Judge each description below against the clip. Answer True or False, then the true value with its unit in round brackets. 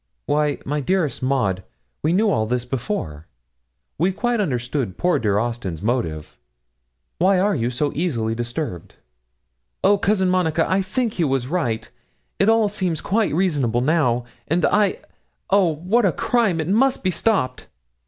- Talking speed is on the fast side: False (155 wpm)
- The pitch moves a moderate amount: False (8.0 semitones)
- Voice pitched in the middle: True (160 Hz)